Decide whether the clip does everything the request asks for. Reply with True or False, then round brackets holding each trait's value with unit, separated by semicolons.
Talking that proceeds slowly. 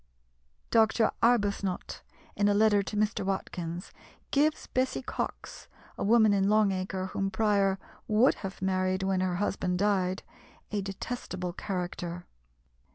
True (130 wpm)